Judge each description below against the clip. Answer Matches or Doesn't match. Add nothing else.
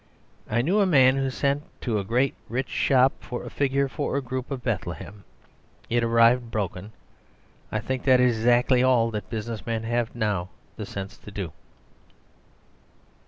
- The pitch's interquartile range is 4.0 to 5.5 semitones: Doesn't match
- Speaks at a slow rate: Doesn't match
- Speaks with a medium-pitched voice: Doesn't match